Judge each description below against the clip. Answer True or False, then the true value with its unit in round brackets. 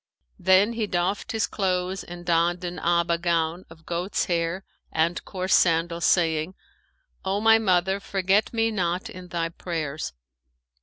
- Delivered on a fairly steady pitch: True (2.2 semitones)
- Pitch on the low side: False (180 Hz)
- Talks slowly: False (145 wpm)